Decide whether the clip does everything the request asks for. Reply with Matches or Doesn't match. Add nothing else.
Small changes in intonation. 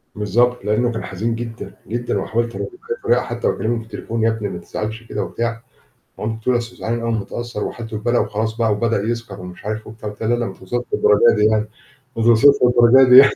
Matches